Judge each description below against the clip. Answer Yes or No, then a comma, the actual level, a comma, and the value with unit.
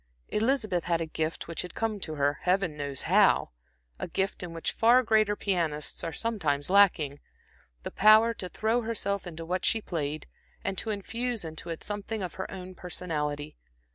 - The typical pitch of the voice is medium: Yes, medium, 180 Hz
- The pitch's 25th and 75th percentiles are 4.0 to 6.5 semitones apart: Yes, average, 5.1 semitones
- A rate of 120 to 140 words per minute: No, average, 175 wpm